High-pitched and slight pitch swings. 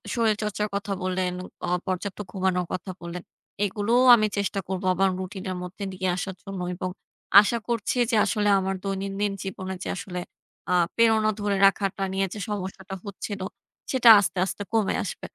Yes: high, 195 Hz; narrow, 1.9 semitones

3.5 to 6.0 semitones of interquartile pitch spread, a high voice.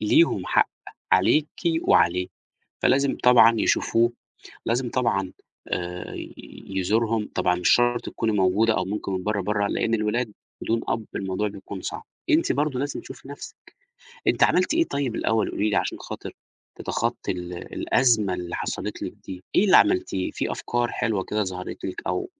No: average, 4.3 semitones; low, 110 Hz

